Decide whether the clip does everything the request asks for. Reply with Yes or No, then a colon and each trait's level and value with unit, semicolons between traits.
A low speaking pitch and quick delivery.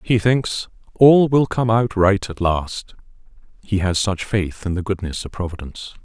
No: low, 100 Hz; average, 180 wpm